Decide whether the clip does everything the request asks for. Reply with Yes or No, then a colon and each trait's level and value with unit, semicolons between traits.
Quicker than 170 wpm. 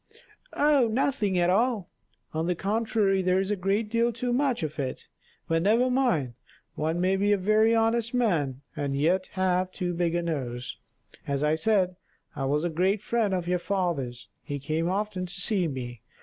Yes: average, 185 wpm